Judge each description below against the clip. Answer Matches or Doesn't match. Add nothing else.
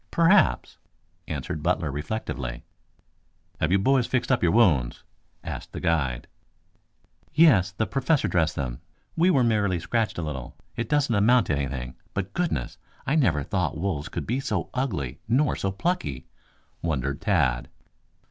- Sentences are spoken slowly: Doesn't match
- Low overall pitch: Matches